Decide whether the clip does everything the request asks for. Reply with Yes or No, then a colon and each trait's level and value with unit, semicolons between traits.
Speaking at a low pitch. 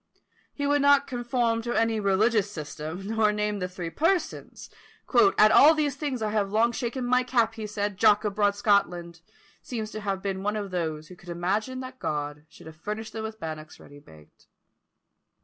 No: high, 210 Hz